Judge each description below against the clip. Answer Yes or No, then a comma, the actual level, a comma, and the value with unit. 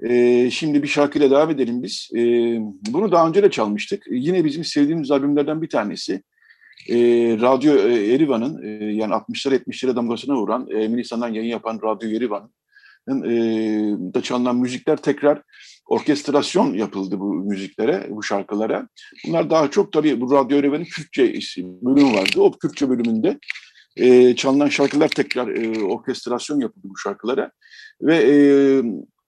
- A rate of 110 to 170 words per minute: Yes, average, 125 wpm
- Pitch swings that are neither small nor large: Yes, average, 4.5 semitones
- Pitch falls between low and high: No, low, 130 Hz